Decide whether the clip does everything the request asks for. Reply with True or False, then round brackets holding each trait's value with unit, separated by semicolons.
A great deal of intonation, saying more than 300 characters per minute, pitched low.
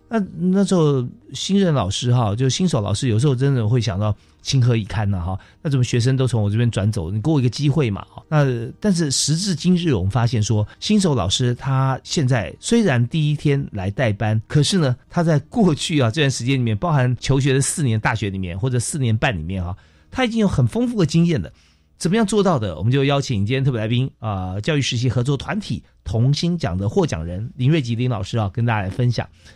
True (5.7 semitones; 340 characters per minute; 130 Hz)